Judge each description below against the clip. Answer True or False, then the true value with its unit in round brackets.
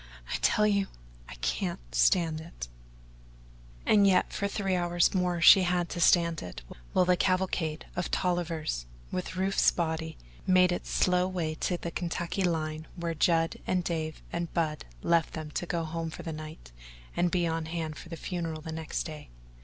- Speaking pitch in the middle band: True (170 Hz)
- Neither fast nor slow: True (175 wpm)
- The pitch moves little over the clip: True (2.3 semitones)